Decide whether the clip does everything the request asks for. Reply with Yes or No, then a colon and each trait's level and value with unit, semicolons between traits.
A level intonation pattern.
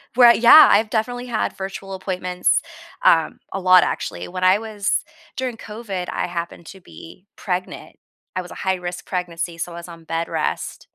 No: average, 3.4 semitones